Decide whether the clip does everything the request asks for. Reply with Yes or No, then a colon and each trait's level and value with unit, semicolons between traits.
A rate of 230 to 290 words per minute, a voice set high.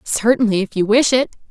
No: average, 200 wpm; high, 225 Hz